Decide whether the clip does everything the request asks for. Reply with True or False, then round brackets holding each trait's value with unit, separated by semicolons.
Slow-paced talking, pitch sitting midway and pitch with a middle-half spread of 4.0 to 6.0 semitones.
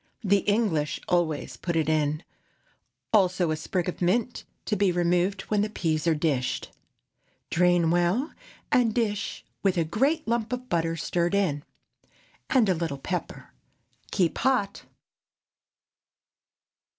True (130 wpm; 180 Hz; 4.3 semitones)